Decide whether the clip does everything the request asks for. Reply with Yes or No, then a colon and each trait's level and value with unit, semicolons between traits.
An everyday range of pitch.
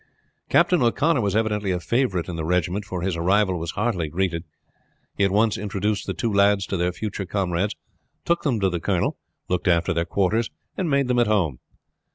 Yes: average, 3.7 semitones